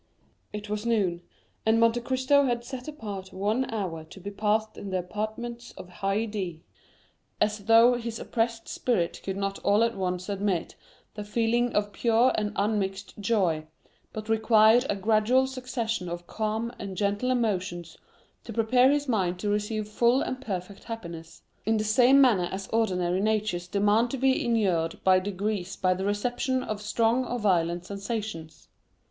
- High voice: Yes, high, 215 Hz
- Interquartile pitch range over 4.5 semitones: No, average, 3.4 semitones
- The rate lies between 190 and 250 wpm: No, average, 160 wpm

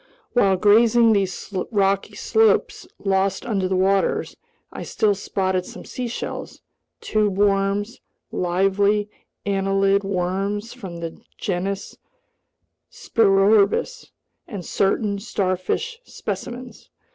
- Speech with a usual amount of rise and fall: No, narrow, 1.9 semitones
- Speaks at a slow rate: Yes, slow, 95 wpm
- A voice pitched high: Yes, high, 200 Hz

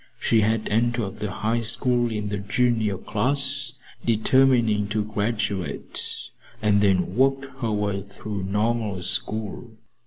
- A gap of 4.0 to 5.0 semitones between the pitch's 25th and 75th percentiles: No, narrow, 2.6 semitones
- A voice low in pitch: Yes, low, 110 Hz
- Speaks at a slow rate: Yes, slow, 130 wpm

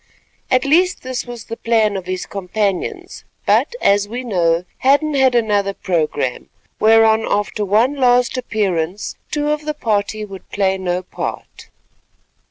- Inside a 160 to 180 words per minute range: No, average, 145 wpm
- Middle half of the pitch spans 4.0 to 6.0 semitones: Yes, average, 4.8 semitones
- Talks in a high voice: Yes, high, 215 Hz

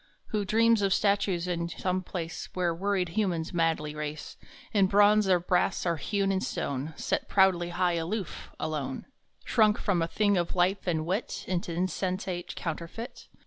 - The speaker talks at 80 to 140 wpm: No, average, 160 wpm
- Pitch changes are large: No, average, 3.0 semitones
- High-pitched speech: No, medium, 180 Hz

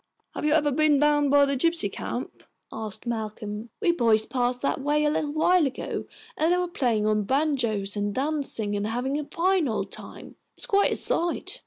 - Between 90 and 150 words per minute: No, average, 195 wpm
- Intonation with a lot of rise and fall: Yes, wide, 5.7 semitones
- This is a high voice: Yes, very high, 280 Hz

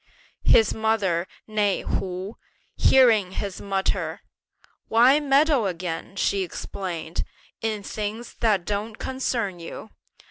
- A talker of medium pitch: No, high, 205 Hz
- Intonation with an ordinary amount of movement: Yes, average, 3.1 semitones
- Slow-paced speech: Yes, slow, 105 wpm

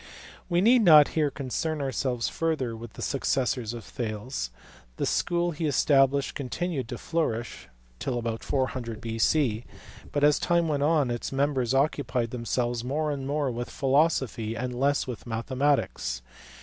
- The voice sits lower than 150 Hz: Yes, low, 135 Hz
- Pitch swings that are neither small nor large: Yes, average, 3.8 semitones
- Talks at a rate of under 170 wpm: Yes, average, 150 wpm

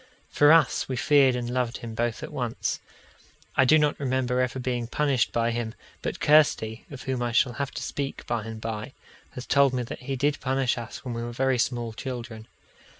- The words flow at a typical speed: No, fast, 210 wpm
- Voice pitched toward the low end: Yes, low, 125 Hz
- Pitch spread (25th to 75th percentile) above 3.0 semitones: No, narrow, 2.4 semitones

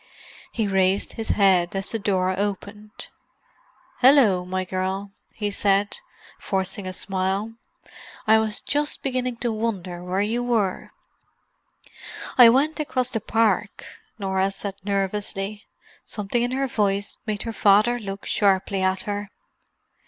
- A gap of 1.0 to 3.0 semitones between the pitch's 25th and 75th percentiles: Yes, average, 2.7 semitones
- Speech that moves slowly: Yes, slow, 130 wpm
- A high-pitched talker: Yes, high, 205 Hz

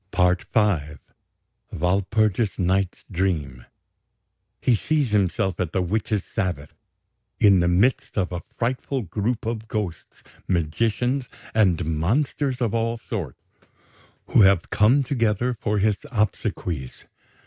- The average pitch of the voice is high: No, low, 100 Hz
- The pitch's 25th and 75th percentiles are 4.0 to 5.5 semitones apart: Yes, average, 4.4 semitones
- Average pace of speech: No, slow, 115 wpm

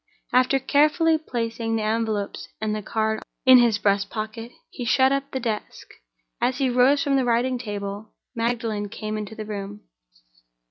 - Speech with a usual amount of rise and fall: Yes, average, 3.2 semitones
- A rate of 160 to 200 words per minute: Yes, average, 165 wpm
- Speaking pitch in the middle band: No, high, 230 Hz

